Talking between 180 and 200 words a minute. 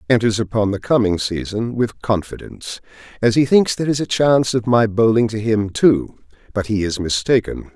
Yes: average, 185 wpm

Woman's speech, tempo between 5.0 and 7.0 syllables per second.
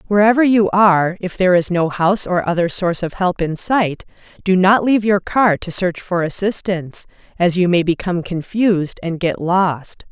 Yes: female; 5.2 syllables/s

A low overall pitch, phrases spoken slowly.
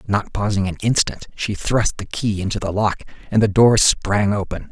No: low, 105 Hz; fast, 205 wpm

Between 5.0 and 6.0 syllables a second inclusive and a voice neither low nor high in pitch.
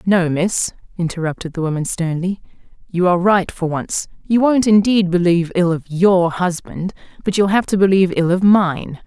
Yes: 5.1 syllables/s; medium, 180 Hz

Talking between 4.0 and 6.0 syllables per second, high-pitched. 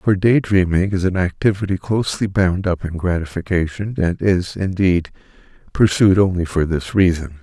No: 4.9 syllables/s; very low, 90 Hz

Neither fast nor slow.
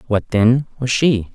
Yes: average, 180 wpm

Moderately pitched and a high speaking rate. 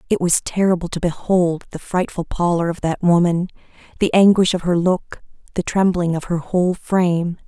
No: medium, 175 Hz; average, 175 wpm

